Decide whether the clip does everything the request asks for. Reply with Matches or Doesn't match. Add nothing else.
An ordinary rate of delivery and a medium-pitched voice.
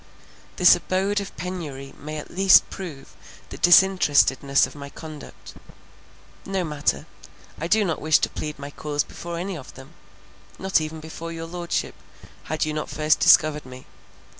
Matches